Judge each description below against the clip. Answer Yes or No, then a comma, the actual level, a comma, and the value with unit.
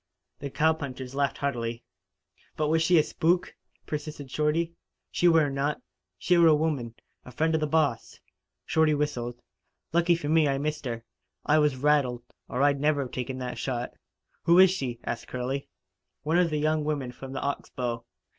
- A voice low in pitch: No, medium, 145 Hz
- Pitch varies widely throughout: No, average, 3.6 semitones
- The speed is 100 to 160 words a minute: No, average, 175 wpm